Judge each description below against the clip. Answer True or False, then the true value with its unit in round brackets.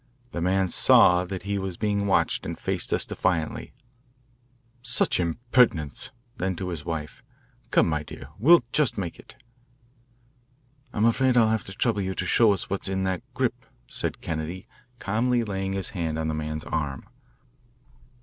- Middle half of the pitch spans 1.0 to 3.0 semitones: False (4.5 semitones)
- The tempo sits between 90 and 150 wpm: False (160 wpm)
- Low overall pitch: True (95 Hz)